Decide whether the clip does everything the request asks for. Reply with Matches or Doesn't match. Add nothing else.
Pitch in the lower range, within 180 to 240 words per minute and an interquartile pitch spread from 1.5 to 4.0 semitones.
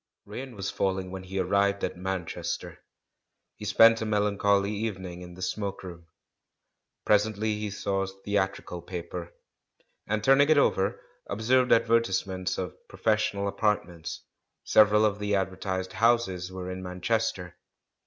Doesn't match